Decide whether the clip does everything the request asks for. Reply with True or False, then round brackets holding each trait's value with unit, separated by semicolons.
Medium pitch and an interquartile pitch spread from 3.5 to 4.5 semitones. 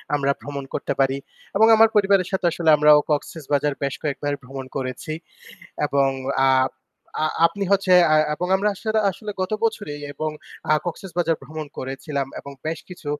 False (155 Hz; 5.1 semitones)